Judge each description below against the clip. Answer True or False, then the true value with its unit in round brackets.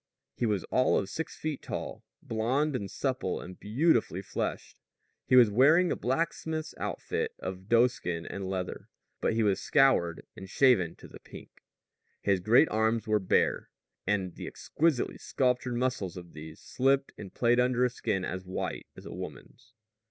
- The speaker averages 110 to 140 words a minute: False (165 wpm)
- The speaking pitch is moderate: False (115 Hz)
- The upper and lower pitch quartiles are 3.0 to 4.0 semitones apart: False (5.3 semitones)